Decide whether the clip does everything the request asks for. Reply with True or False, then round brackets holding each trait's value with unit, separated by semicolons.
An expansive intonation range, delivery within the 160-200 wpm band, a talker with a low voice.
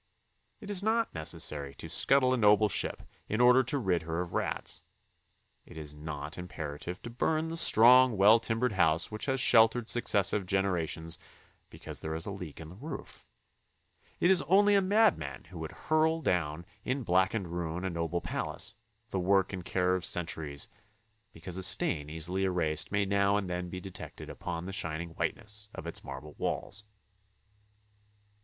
True (6.0 semitones; 170 wpm; 95 Hz)